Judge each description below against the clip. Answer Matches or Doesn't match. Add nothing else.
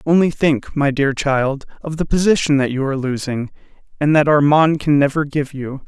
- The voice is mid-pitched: Matches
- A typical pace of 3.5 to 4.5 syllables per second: Doesn't match